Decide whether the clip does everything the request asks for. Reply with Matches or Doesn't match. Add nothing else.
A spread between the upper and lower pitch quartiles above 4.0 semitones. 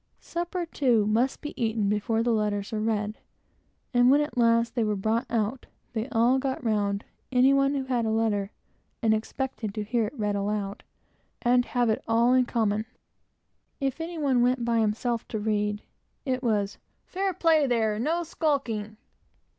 Doesn't match